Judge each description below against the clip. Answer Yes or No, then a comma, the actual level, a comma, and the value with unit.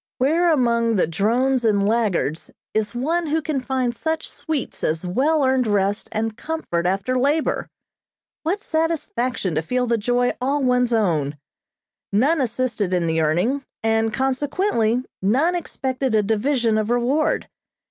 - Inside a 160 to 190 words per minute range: No, average, 145 wpm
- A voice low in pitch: No, high, 245 Hz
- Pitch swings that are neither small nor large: Yes, average, 4.8 semitones